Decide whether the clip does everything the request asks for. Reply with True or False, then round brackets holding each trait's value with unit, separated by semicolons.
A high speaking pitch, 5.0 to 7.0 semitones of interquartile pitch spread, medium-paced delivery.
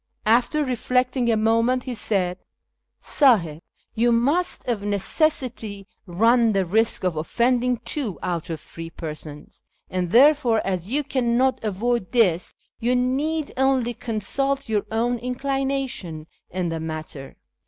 False (230 Hz; 5.4 semitones; 130 wpm)